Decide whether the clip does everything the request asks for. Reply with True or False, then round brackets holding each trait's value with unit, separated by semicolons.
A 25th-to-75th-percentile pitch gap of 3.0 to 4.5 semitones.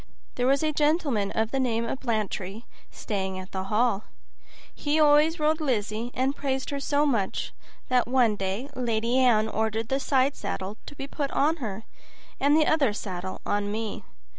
False (4.9 semitones)